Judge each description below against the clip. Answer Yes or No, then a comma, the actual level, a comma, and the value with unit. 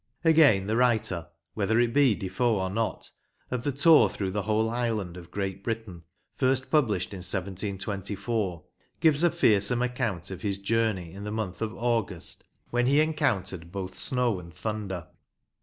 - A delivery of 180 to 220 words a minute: No, average, 160 wpm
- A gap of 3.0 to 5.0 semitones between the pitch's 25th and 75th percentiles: Yes, average, 4.3 semitones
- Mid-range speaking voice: No, low, 105 Hz